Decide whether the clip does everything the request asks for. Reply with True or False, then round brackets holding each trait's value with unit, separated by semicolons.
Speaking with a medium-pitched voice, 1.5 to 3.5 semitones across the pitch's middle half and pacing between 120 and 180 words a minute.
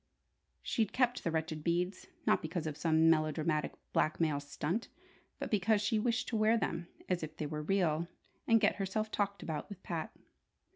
False (170 Hz; 5.1 semitones; 175 wpm)